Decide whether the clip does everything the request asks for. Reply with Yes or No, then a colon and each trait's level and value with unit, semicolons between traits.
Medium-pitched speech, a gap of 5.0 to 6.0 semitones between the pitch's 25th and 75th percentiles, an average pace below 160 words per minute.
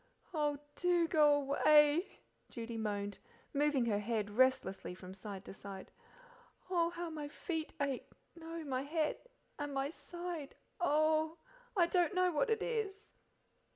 No: very high, 295 Hz; wide, 5.5 semitones; average, 140 wpm